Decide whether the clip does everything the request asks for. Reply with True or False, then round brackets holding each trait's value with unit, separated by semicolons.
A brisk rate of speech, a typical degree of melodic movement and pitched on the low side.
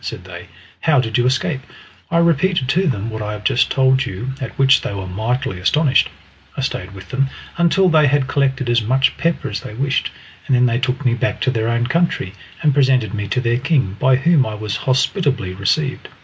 True (215 wpm; 4.2 semitones; 130 Hz)